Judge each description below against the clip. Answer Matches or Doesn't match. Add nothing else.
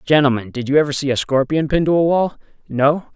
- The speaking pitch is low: Doesn't match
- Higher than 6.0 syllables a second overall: Matches